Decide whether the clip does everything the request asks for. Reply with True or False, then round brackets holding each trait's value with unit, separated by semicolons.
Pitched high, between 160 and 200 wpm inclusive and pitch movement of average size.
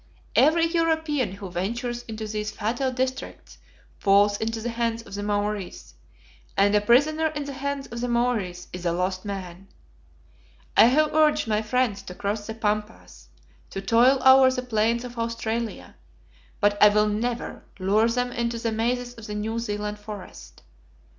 True (225 Hz; 165 wpm; 3.2 semitones)